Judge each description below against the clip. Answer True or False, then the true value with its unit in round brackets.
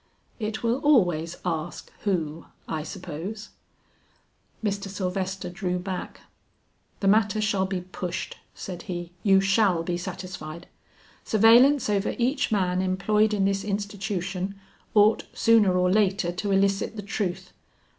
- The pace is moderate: False (125 wpm)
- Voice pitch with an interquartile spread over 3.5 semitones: False (2.7 semitones)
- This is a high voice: True (195 Hz)